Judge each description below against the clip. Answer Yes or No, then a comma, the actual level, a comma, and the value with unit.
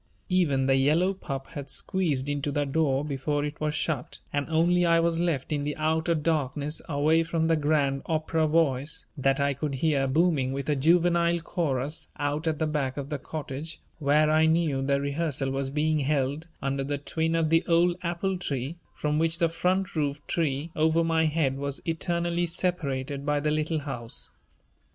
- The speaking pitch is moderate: Yes, medium, 150 Hz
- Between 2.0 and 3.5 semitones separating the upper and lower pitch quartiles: Yes, average, 2.8 semitones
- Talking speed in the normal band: Yes, average, 185 wpm